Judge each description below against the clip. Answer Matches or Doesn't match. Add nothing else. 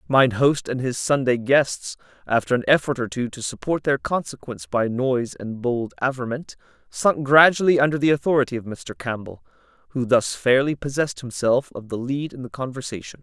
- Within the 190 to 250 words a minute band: Doesn't match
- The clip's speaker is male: Matches